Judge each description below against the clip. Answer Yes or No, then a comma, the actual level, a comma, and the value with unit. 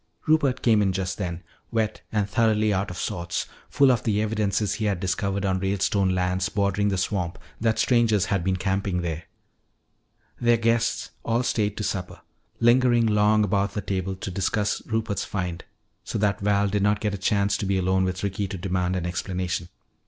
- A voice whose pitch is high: No, low, 100 Hz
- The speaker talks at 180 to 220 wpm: Yes, average, 185 wpm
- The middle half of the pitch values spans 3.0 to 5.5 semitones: No, narrow, 2.5 semitones